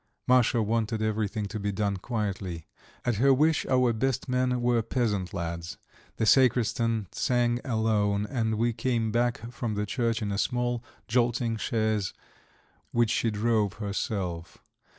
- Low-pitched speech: Yes, low, 115 Hz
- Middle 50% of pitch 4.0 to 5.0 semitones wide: No, average, 2.7 semitones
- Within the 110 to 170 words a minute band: Yes, average, 145 wpm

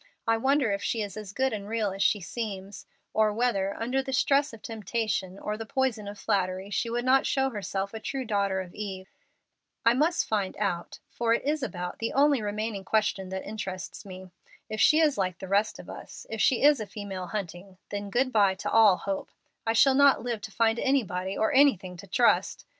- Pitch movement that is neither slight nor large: Yes, average, 3.7 semitones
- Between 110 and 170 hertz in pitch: No, high, 215 Hz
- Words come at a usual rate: No, fast, 210 wpm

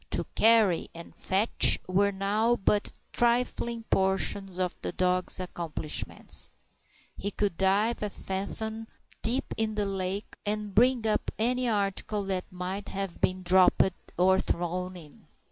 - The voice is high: Yes, high, 195 Hz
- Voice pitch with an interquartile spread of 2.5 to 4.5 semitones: Yes, average, 2.9 semitones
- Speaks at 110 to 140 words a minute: Yes, slow, 135 wpm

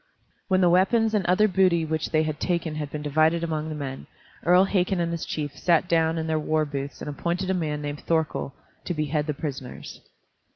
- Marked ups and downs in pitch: No, average, 2.8 semitones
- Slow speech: No, fast, 205 wpm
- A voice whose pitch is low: No, medium, 160 Hz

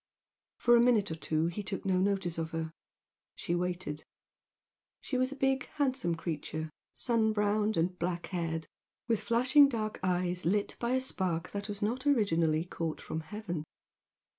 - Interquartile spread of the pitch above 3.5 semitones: Yes, wide, 5.6 semitones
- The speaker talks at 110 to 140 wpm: No, average, 165 wpm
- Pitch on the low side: No, high, 190 Hz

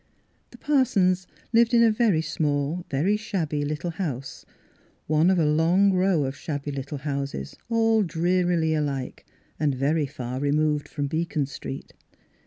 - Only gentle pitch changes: No, average, 4.3 semitones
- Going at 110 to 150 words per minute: Yes, average, 145 wpm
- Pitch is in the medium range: Yes, medium, 155 Hz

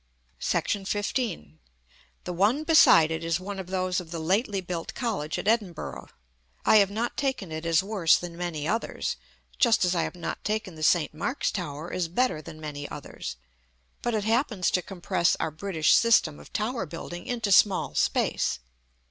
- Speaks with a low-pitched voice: No, medium, 185 Hz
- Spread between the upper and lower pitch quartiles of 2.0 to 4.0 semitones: No, average, 4.6 semitones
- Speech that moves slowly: No, average, 175 wpm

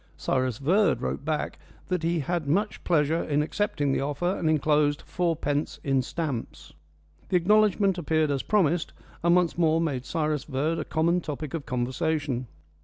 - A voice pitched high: No, medium, 155 Hz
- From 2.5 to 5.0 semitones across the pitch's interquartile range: Yes, average, 3.3 semitones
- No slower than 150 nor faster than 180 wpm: Yes, average, 160 wpm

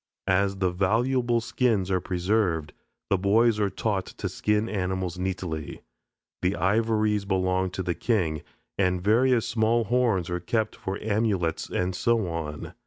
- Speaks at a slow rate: No, average, 145 wpm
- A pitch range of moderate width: Yes, average, 3.5 semitones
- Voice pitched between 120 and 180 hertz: No, low, 100 Hz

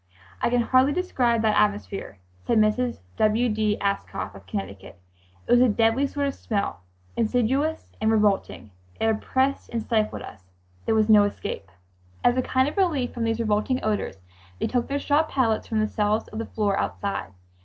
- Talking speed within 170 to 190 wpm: Yes, average, 180 wpm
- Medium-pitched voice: No, high, 220 Hz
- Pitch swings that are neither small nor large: Yes, average, 3.4 semitones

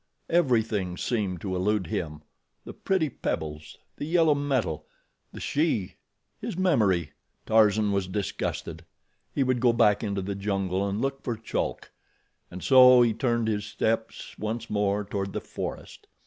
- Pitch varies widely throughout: No, average, 4.2 semitones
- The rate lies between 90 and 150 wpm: Yes, average, 145 wpm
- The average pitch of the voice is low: Yes, low, 105 Hz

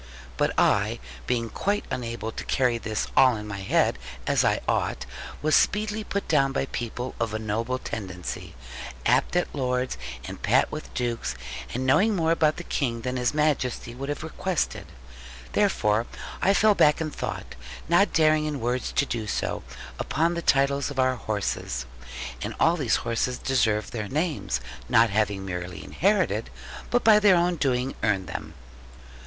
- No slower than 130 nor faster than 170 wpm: Yes, average, 165 wpm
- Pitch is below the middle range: Yes, low, 130 Hz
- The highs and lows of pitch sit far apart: Yes, wide, 5.8 semitones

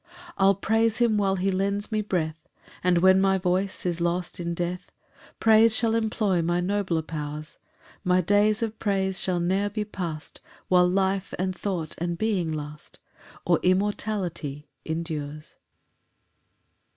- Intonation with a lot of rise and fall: No, average, 3.1 semitones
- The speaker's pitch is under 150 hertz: No, medium, 185 Hz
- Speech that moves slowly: No, average, 145 wpm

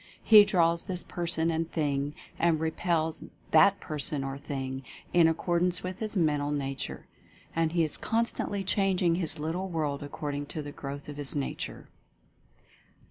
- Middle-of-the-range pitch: Yes, medium, 160 Hz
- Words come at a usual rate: Yes, average, 150 wpm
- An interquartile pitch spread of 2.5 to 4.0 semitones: Yes, average, 3.4 semitones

